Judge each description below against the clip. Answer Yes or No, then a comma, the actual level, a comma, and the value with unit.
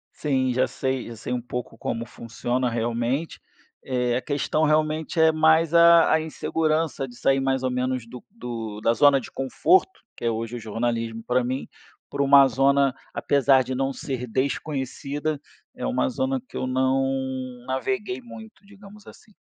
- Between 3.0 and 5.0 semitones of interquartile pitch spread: Yes, average, 3.9 semitones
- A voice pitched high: No, low, 130 Hz